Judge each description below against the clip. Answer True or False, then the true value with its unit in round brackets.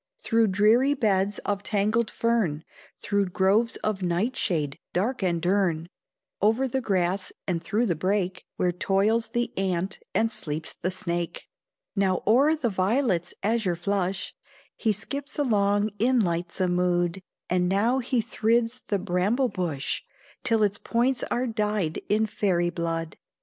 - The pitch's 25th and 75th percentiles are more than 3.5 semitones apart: True (4.1 semitones)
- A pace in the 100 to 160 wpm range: True (140 wpm)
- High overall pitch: True (200 Hz)